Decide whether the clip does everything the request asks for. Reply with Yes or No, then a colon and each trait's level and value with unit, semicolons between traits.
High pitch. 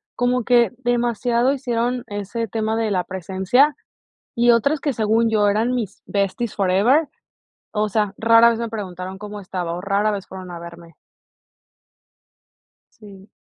Yes: high, 215 Hz